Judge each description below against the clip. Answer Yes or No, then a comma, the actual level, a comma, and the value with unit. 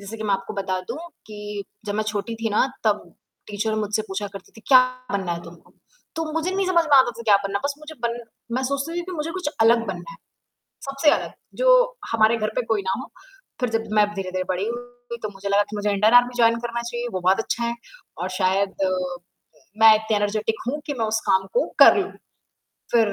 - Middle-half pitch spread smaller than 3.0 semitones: No, average, 3.5 semitones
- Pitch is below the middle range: No, high, 220 Hz